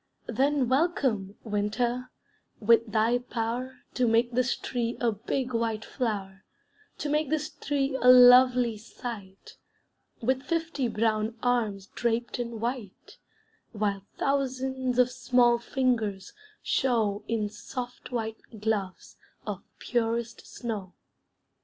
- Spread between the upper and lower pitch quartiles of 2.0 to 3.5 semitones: Yes, average, 2.7 semitones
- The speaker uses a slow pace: Yes, slow, 115 wpm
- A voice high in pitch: Yes, high, 240 Hz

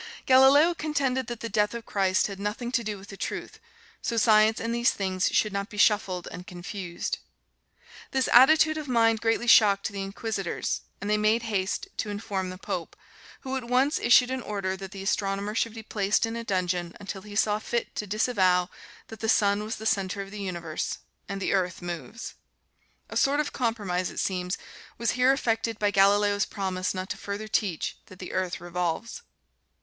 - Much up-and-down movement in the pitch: No, average, 3.3 semitones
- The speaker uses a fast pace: No, average, 190 wpm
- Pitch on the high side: Yes, high, 210 Hz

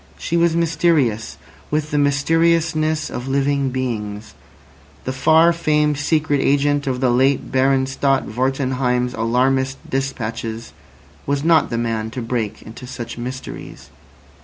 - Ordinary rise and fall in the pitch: Yes, average, 3.3 semitones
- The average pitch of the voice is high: No, low, 135 Hz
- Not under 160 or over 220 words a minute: No, slow, 135 wpm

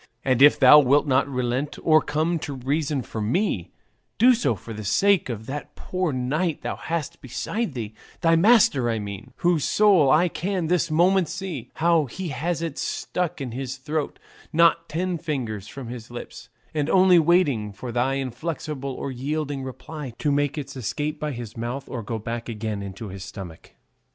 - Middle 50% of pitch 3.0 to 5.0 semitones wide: No, wide, 5.5 semitones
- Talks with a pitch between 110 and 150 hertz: Yes, medium, 140 Hz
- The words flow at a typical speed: Yes, average, 180 wpm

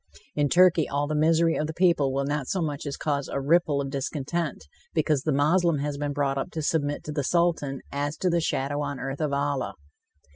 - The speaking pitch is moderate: Yes, medium, 145 Hz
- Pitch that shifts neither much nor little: No, narrow, 2.3 semitones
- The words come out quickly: Yes, fast, 220 wpm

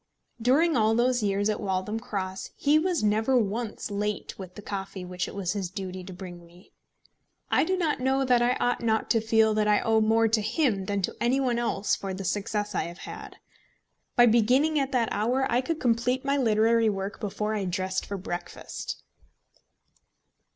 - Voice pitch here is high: Yes, high, 220 Hz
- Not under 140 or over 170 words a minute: No, average, 195 wpm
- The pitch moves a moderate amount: Yes, average, 3.9 semitones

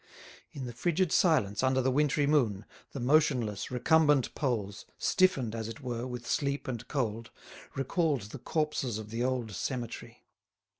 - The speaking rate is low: No, average, 150 wpm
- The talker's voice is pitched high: No, low, 130 Hz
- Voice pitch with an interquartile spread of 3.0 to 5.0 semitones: Yes, average, 4.2 semitones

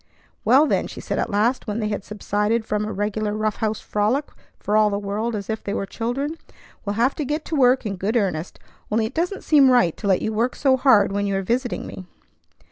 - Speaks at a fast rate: Yes, fast, 235 wpm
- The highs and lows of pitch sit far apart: No, average, 3.6 semitones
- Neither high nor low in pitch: No, high, 215 Hz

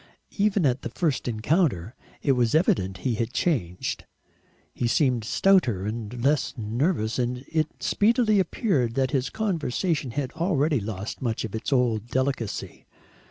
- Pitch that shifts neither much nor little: No, wide, 6.0 semitones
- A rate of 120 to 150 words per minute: Yes, average, 145 wpm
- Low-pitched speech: Yes, low, 130 Hz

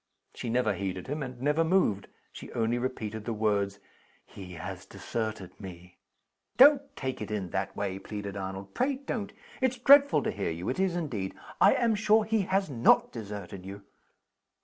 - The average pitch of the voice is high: No, low, 110 Hz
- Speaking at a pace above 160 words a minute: Yes, average, 170 wpm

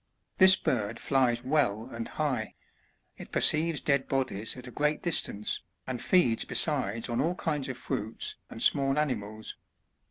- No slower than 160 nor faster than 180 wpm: No, average, 150 wpm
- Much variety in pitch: No, average, 4.7 semitones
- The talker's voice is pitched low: Yes, low, 130 Hz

